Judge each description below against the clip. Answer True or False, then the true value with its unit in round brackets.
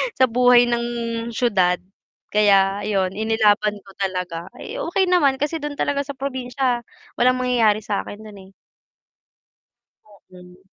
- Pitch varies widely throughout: False (4.4 semitones)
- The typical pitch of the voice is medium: False (220 Hz)